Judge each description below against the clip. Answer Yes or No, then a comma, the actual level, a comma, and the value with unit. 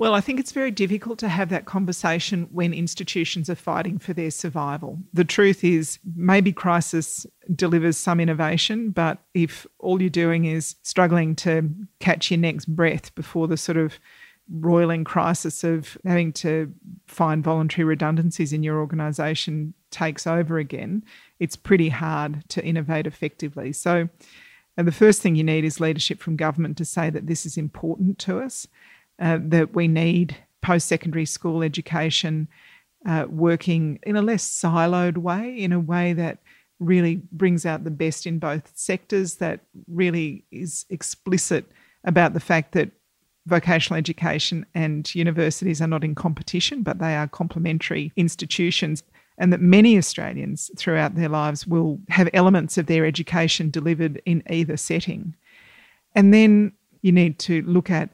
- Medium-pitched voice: Yes, medium, 170 Hz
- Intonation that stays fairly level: Yes, narrow, 2.1 semitones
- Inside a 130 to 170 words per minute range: Yes, average, 155 wpm